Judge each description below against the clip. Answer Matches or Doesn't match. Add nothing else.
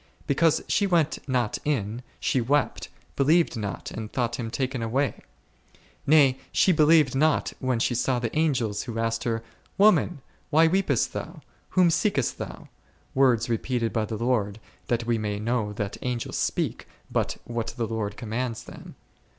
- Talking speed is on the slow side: Doesn't match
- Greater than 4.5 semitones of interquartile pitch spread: Doesn't match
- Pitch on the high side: Doesn't match